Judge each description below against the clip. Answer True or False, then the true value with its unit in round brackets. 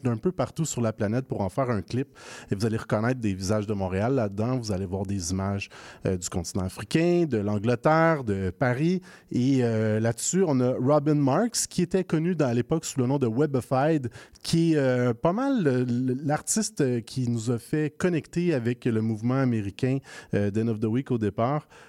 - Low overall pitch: True (125 Hz)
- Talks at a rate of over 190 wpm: True (200 wpm)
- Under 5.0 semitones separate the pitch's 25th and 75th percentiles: False (5.5 semitones)